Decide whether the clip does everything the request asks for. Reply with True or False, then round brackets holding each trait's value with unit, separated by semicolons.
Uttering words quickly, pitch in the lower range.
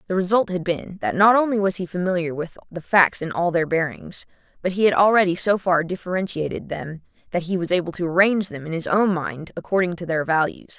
False (225 wpm; 180 Hz)